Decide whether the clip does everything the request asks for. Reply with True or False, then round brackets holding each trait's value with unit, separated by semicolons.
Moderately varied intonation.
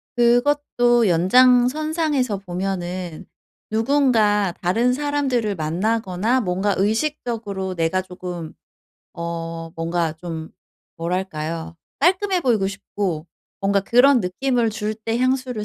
False (5.8 semitones)